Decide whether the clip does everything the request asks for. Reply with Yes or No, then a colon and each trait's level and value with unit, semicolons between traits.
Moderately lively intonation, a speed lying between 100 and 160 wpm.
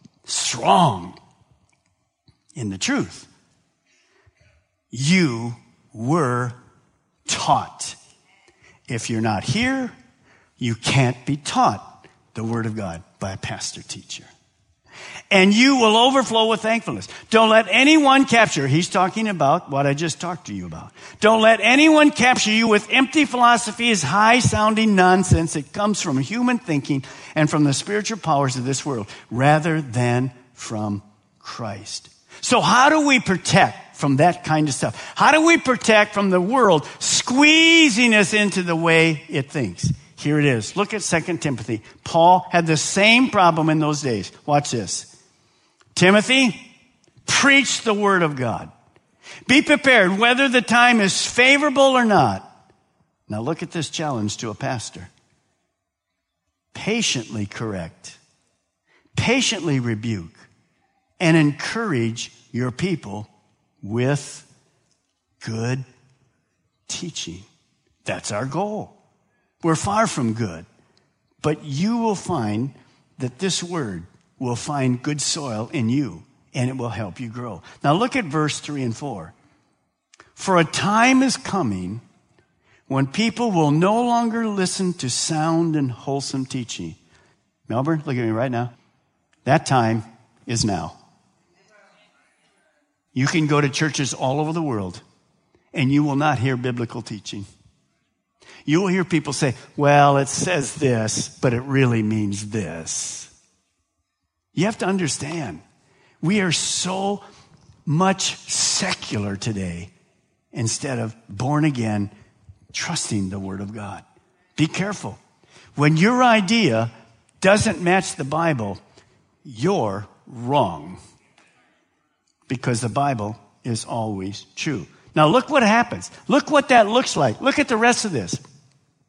No: wide, 8.9 semitones; slow, 135 wpm